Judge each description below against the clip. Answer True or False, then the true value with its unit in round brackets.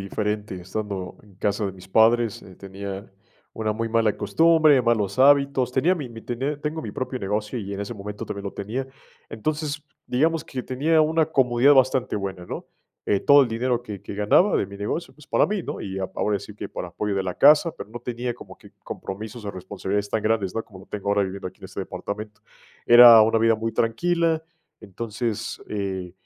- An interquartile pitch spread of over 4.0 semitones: True (4.5 semitones)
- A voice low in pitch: True (110 Hz)